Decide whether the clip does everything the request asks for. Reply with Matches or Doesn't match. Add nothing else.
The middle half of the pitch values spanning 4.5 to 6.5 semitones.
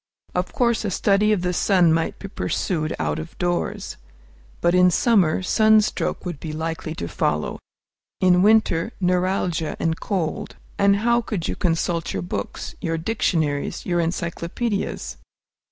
Doesn't match